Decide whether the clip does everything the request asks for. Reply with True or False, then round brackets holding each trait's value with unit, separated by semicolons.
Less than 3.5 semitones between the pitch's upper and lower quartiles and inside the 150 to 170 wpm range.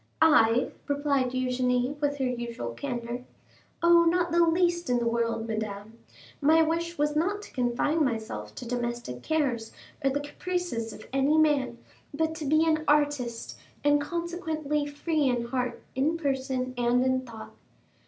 False (4.6 semitones; 155 wpm)